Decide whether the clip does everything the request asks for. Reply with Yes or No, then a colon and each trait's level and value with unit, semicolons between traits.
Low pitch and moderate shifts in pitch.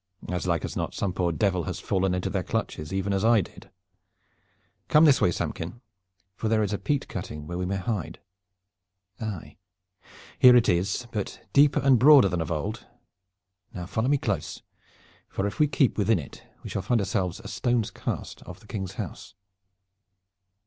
Yes: low, 100 Hz; average, 4.3 semitones